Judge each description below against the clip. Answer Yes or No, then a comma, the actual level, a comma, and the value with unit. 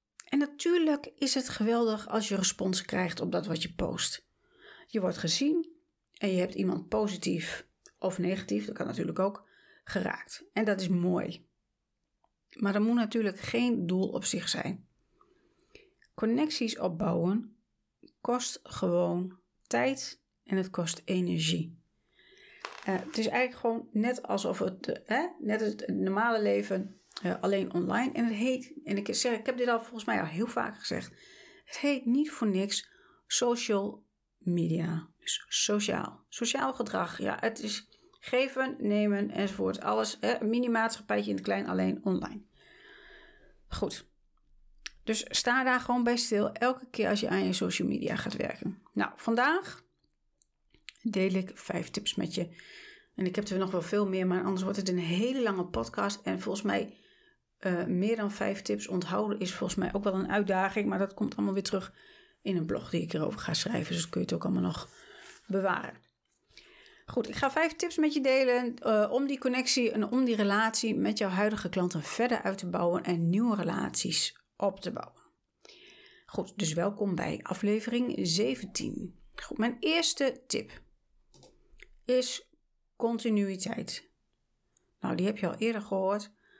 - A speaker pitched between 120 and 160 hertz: No, high, 215 Hz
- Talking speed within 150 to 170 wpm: Yes, average, 165 wpm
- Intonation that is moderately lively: Yes, average, 5.0 semitones